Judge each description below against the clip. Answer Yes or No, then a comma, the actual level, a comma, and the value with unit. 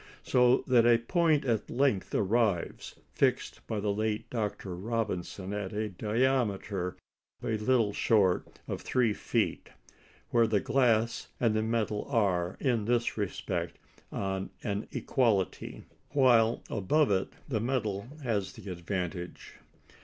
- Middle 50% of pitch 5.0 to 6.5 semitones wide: No, average, 3.3 semitones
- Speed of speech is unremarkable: No, slow, 130 wpm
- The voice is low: Yes, low, 110 Hz